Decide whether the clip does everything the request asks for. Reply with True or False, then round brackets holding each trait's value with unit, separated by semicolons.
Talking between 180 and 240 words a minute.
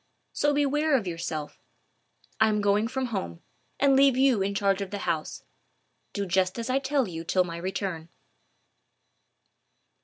False (155 wpm)